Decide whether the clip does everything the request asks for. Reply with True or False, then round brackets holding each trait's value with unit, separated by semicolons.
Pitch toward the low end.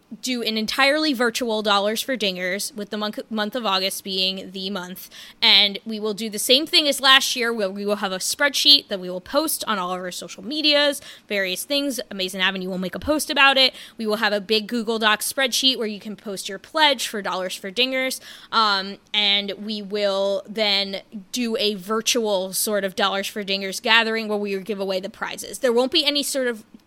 False (215 Hz)